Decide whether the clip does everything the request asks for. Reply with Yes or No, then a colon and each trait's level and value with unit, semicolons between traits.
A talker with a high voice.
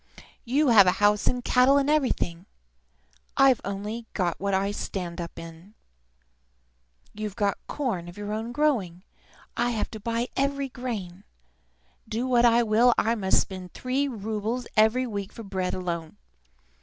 Yes: high, 215 Hz